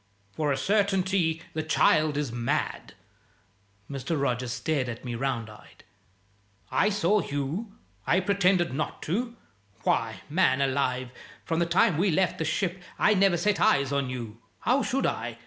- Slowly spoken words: No, average, 155 wpm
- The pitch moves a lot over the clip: Yes, wide, 6.5 semitones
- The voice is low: No, medium, 155 Hz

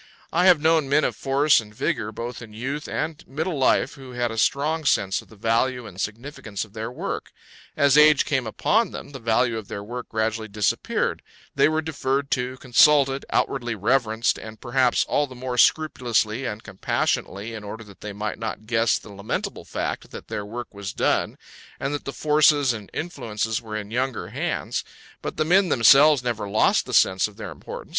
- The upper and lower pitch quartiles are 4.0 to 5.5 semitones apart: Yes, average, 4.4 semitones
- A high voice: No, low, 120 Hz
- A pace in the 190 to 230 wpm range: Yes, average, 195 wpm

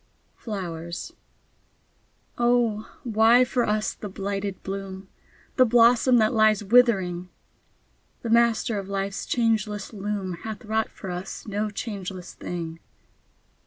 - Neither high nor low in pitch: No, high, 210 Hz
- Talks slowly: Yes, slow, 115 wpm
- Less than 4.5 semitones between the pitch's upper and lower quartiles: Yes, average, 3.0 semitones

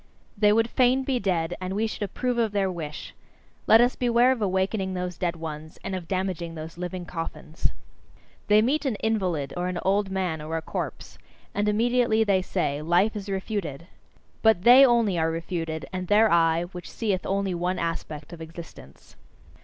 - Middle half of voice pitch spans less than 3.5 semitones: No, average, 4.4 semitones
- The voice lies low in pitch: No, medium, 185 Hz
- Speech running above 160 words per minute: Yes, average, 180 wpm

